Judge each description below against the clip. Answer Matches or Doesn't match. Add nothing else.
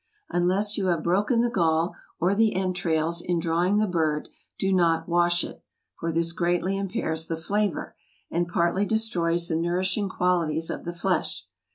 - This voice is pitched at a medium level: Matches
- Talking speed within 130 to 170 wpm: Matches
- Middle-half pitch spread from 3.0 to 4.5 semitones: Doesn't match